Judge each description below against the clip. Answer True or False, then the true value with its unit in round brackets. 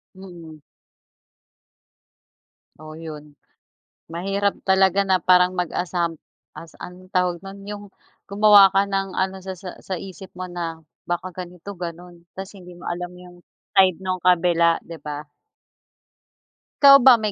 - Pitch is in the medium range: True (180 Hz)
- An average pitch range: False (1.9 semitones)